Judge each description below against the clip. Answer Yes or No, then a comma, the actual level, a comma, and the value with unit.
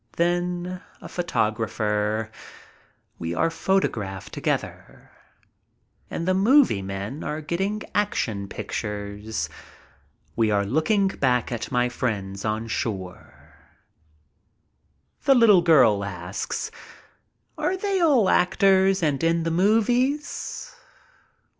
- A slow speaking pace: Yes, slow, 100 wpm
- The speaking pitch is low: No, medium, 155 Hz